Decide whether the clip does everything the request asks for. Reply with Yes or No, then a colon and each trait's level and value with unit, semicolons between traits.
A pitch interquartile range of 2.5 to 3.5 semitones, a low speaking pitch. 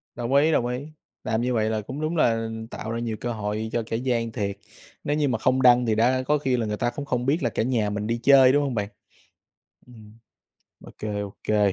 Yes: average, 3.0 semitones; low, 120 Hz